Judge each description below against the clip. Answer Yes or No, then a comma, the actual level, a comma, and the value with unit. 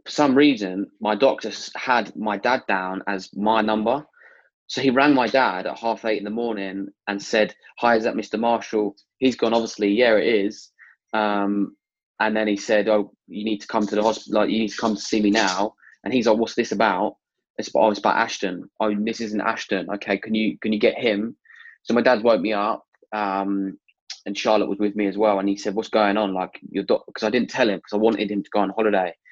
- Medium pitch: No, low, 105 Hz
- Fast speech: Yes, fast, 240 wpm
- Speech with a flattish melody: Yes, narrow, 1.7 semitones